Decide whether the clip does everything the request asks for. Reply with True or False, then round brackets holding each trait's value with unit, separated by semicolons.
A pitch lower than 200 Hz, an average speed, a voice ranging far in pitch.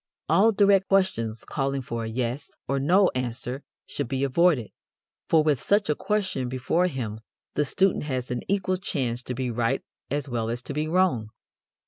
True (135 Hz; 175 wpm; 6.9 semitones)